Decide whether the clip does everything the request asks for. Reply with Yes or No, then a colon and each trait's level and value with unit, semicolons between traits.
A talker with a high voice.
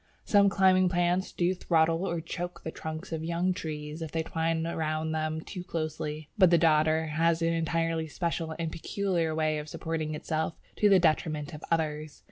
No: medium, 165 Hz